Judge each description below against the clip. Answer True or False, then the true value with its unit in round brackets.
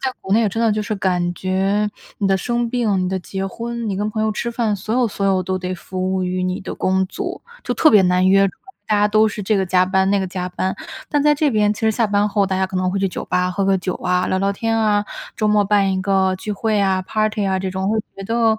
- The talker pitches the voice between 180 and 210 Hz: True (195 Hz)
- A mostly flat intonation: True (2.3 semitones)